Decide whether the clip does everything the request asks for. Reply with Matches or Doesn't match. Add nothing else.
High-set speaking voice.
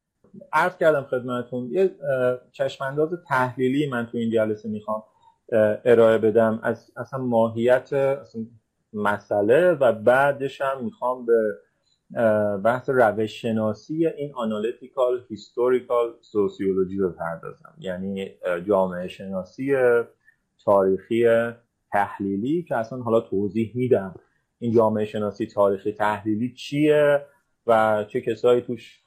Doesn't match